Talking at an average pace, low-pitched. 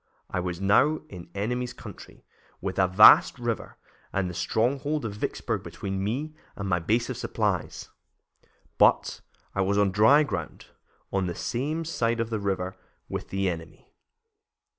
Yes: average, 160 wpm; low, 105 Hz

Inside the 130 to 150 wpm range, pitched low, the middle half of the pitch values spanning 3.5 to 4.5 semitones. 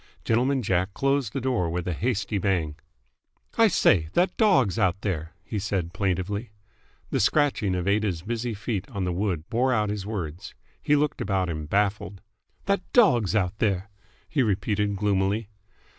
No: average, 160 wpm; low, 100 Hz; average, 4.1 semitones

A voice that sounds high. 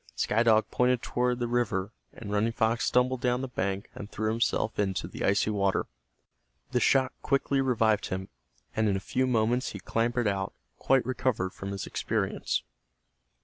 No: low, 115 Hz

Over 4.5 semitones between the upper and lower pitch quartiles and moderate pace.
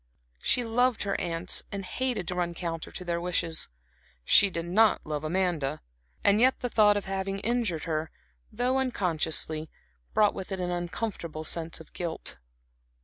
No: average, 4.1 semitones; average, 160 wpm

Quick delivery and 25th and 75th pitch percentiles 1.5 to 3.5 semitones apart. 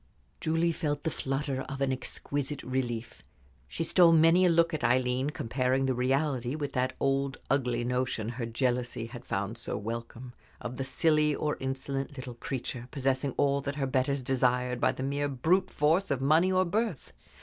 No: average, 175 wpm; average, 3.0 semitones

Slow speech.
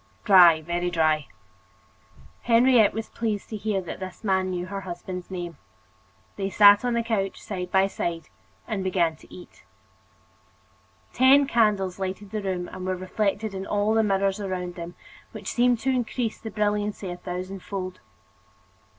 No: average, 160 wpm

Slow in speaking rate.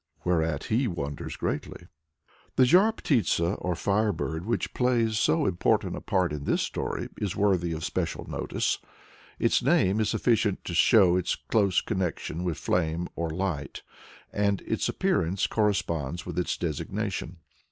No: average, 150 wpm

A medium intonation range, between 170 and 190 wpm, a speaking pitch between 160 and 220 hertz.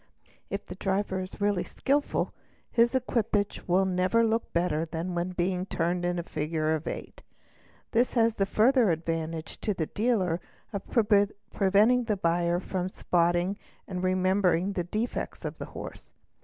No: average, 3.3 semitones; average, 155 wpm; medium, 185 Hz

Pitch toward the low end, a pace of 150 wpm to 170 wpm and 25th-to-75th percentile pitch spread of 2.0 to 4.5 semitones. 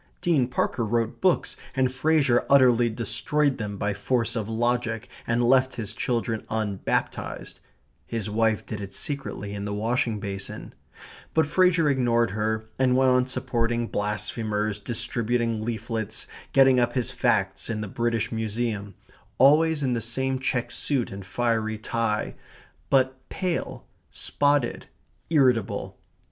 No: low, 115 Hz; slow, 135 wpm; average, 3.2 semitones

